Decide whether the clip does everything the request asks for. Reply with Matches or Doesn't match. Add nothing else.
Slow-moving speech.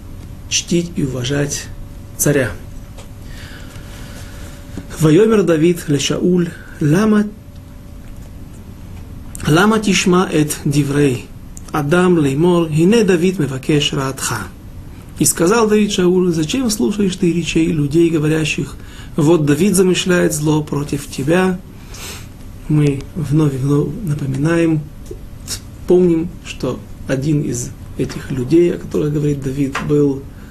Matches